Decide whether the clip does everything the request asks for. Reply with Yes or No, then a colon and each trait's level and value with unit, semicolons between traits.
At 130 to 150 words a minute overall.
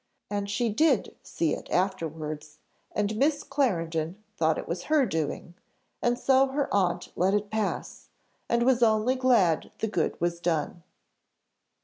Yes: average, 145 wpm